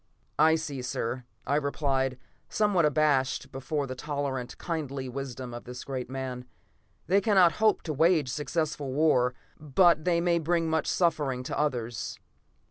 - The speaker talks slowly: No, average, 145 wpm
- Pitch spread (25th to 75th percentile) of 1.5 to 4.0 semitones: Yes, average, 3.7 semitones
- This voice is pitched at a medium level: Yes, medium, 145 Hz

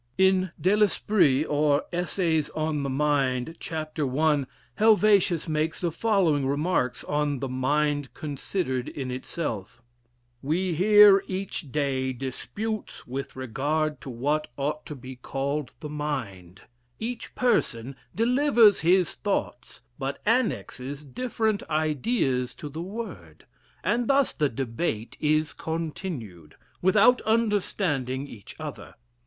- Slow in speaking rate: Yes, slow, 120 wpm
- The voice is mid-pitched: Yes, medium, 150 Hz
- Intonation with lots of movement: Yes, wide, 6.1 semitones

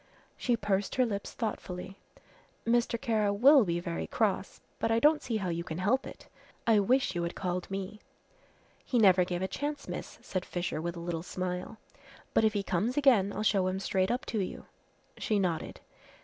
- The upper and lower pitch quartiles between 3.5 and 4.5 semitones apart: Yes, average, 4.1 semitones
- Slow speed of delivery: No, average, 190 wpm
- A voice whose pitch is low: No, high, 195 Hz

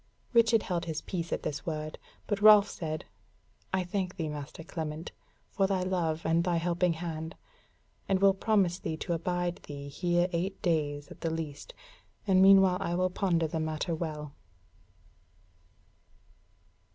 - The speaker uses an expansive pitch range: No, average, 3.0 semitones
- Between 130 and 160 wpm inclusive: Yes, average, 150 wpm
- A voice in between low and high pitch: Yes, medium, 170 Hz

